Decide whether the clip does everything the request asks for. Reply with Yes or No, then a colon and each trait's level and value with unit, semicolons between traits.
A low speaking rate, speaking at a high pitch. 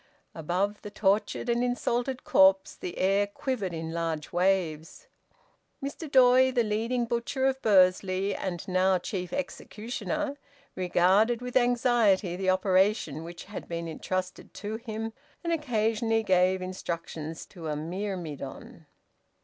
Yes: slow, 125 wpm; high, 195 Hz